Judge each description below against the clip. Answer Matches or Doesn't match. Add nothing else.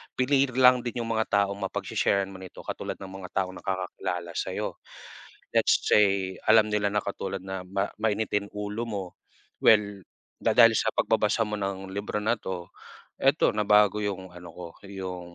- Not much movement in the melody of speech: Matches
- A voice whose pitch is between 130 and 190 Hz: Doesn't match